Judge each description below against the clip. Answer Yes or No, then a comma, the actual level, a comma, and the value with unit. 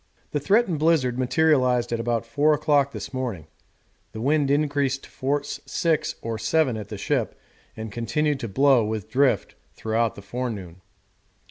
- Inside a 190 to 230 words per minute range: No, average, 155 wpm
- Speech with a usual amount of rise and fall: Yes, average, 4.2 semitones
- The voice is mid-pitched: No, low, 130 Hz